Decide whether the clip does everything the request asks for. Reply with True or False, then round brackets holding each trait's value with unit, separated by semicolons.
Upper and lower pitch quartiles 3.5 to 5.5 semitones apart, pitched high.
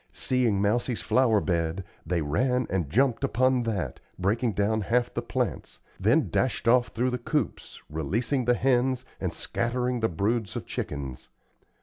False (4.7 semitones; 115 Hz)